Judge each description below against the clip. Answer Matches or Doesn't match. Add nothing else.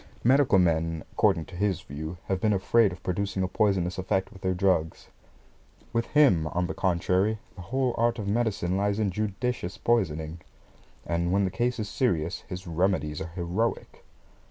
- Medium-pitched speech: Doesn't match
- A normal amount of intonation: Matches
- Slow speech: Doesn't match